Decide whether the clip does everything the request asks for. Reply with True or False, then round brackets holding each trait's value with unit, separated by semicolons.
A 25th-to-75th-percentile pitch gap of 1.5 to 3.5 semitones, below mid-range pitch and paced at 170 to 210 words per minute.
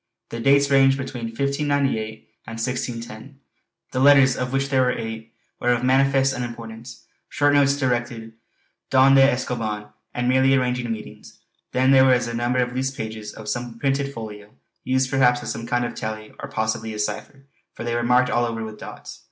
True (2.8 semitones; 125 Hz; 185 wpm)